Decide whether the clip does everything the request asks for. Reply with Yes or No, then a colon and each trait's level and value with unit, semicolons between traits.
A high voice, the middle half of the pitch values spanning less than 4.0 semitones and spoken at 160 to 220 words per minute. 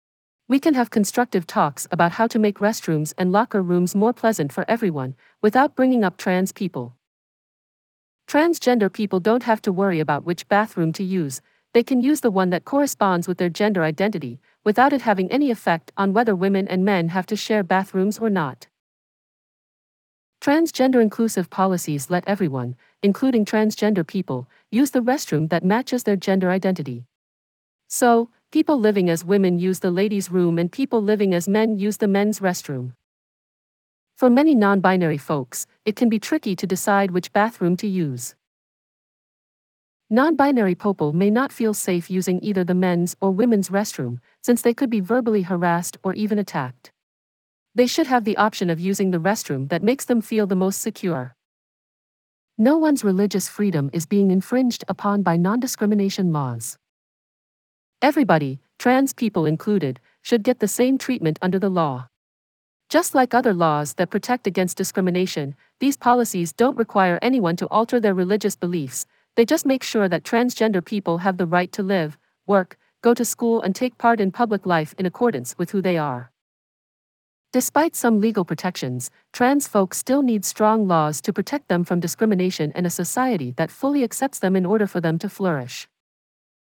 No: high, 195 Hz; average, 4.8 semitones; average, 170 wpm